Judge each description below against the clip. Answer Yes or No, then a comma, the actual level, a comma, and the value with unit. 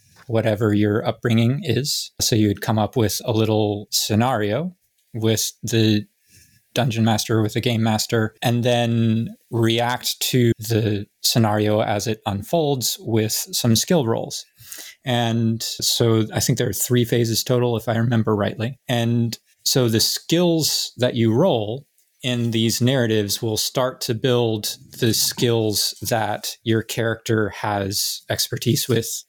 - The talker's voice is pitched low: Yes, low, 115 Hz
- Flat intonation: Yes, narrow, 2.0 semitones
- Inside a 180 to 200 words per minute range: No, average, 140 wpm